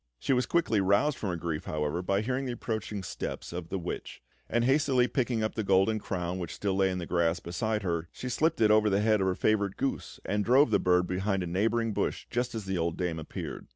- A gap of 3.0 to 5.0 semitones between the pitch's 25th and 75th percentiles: Yes, average, 4.4 semitones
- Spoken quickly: Yes, fast, 240 wpm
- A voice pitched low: Yes, low, 100 Hz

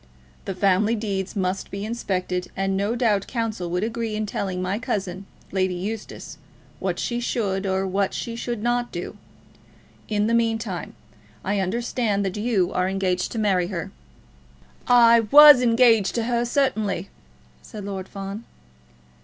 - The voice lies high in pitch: Yes, high, 205 Hz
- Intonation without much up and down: No, average, 3.3 semitones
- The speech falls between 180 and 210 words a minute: No, average, 150 wpm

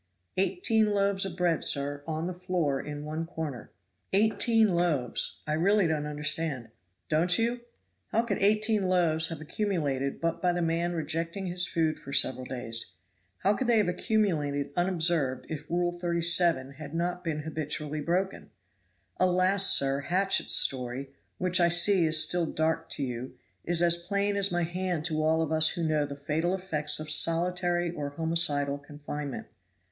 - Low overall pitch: No, medium, 165 Hz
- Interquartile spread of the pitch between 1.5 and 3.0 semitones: No, average, 3.4 semitones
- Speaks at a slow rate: No, average, 160 wpm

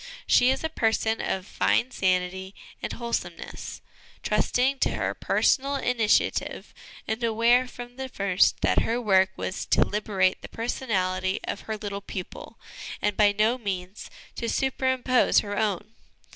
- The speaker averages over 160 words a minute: No, average, 145 wpm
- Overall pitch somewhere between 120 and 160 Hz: No, high, 220 Hz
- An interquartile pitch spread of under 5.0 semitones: Yes, average, 4.2 semitones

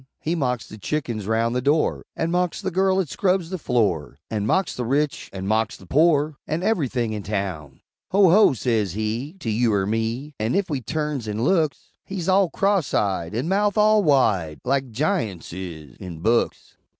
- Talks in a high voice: No, low, 125 Hz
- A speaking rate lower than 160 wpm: No, average, 190 wpm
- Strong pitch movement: Yes, wide, 7.8 semitones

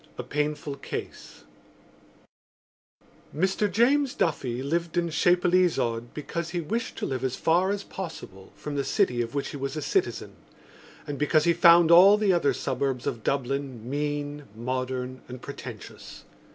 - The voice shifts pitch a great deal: No, average, 4.9 semitones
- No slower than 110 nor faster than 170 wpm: Yes, average, 150 wpm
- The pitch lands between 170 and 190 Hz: No, medium, 150 Hz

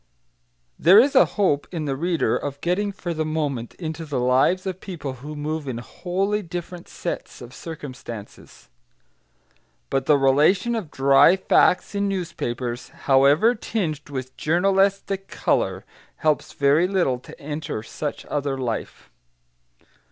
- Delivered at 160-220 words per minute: No, slow, 135 wpm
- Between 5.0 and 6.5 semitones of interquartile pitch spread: Yes, average, 5.3 semitones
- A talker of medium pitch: Yes, medium, 155 Hz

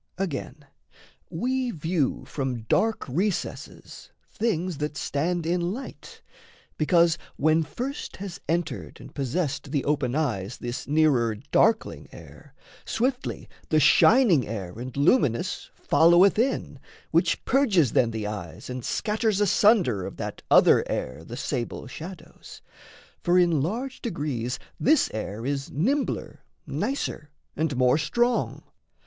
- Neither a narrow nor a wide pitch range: No, wide, 7.4 semitones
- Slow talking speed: Yes, slow, 125 wpm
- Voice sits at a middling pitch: Yes, medium, 155 Hz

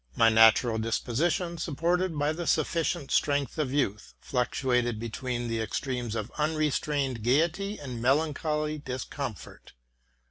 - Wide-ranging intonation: No, average, 4.5 semitones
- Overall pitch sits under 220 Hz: Yes, medium, 140 Hz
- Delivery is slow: Yes, slow, 120 wpm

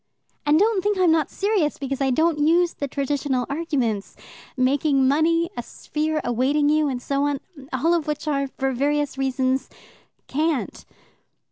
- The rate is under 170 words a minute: Yes, average, 155 wpm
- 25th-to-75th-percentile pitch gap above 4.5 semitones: No, average, 3.0 semitones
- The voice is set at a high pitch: Yes, very high, 290 Hz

